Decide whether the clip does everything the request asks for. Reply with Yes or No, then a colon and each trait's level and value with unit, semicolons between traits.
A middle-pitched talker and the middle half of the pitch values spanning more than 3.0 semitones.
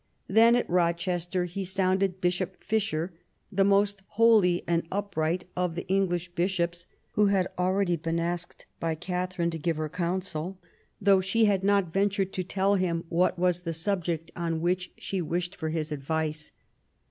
No: medium, 180 Hz; narrow, 2.4 semitones